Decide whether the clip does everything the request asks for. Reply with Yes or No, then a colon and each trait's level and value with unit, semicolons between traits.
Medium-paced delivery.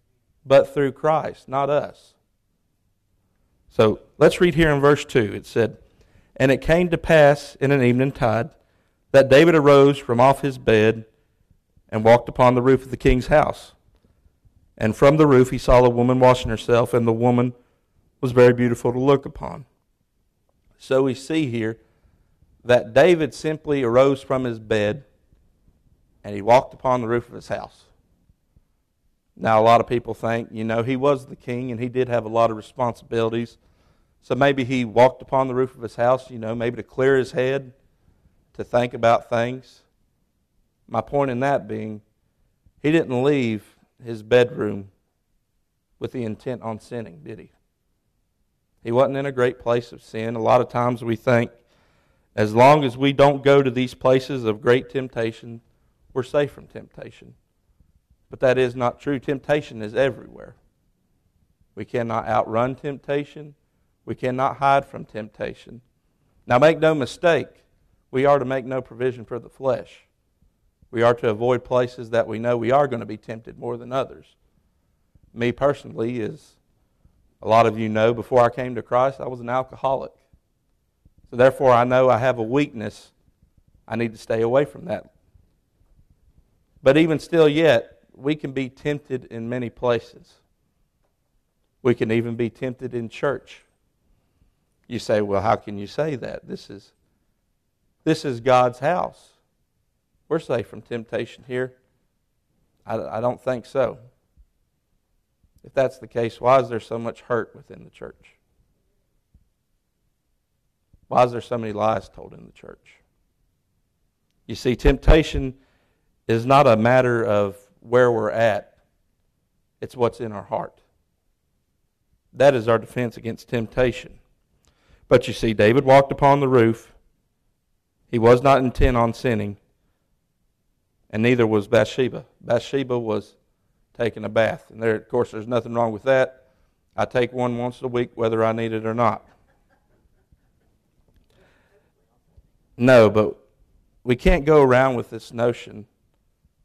Yes: average, 160 wpm